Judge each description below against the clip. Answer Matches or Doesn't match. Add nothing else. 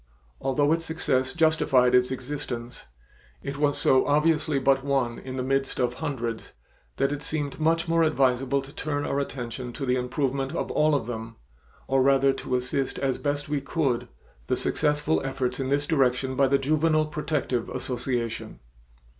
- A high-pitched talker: Doesn't match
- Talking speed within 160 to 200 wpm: Matches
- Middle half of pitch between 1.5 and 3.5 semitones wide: Matches